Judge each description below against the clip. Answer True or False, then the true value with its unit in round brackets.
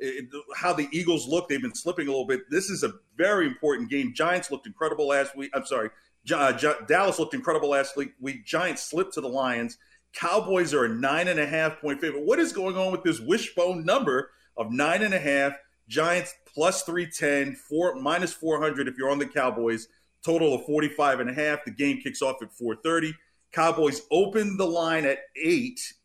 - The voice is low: False (155 Hz)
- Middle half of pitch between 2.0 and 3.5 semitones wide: False (4.3 semitones)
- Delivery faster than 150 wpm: True (200 wpm)